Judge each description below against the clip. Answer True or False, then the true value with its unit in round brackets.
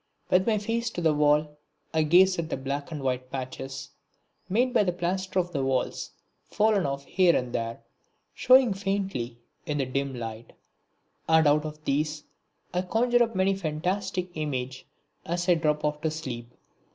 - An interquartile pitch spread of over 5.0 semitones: True (5.5 semitones)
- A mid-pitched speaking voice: True (155 Hz)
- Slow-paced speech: False (175 wpm)